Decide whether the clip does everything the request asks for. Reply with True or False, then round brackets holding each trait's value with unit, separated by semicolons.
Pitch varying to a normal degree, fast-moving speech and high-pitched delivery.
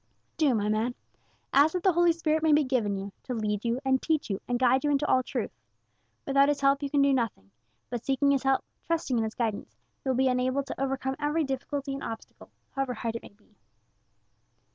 True (3.3 semitones; 220 wpm; 265 Hz)